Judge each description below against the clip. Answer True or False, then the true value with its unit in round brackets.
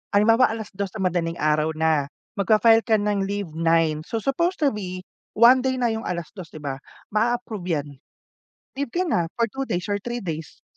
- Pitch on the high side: True (205 Hz)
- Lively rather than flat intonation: True (5.8 semitones)